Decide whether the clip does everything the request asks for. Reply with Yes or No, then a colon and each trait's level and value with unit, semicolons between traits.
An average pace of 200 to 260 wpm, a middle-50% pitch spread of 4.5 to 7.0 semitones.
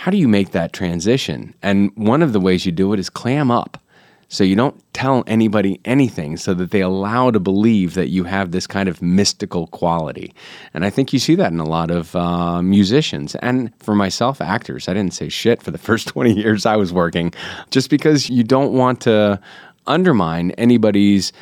Yes: fast, 205 wpm; average, 4.8 semitones